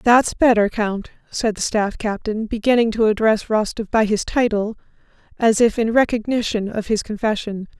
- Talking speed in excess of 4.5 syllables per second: Yes, 4.9 syllables/s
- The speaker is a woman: Yes, female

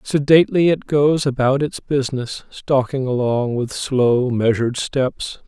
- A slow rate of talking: Yes, slow, 130 wpm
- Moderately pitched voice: No, low, 130 Hz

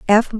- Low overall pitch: No, high, 220 Hz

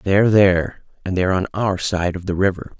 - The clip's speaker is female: No, male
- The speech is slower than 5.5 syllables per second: No, 5.8 syllables/s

